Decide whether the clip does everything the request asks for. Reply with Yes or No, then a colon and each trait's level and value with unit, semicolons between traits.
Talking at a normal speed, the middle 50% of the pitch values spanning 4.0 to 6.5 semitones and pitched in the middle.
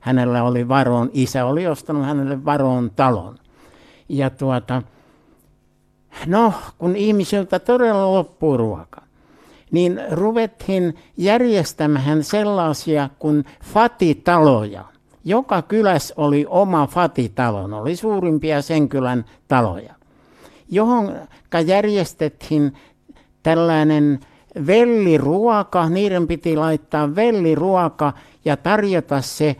No: slow, 90 wpm; average, 5.2 semitones; medium, 155 Hz